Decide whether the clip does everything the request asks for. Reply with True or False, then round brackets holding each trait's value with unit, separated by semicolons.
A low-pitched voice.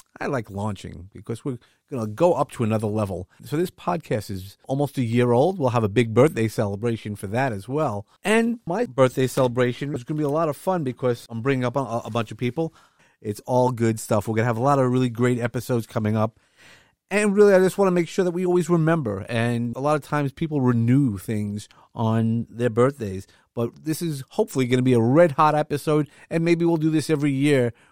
True (125 Hz)